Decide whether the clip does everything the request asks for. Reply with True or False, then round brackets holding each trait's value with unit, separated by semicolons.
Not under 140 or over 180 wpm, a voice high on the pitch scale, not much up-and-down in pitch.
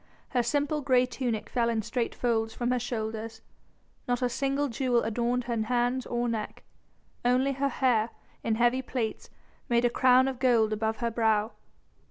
True (170 wpm; 240 Hz; 2.1 semitones)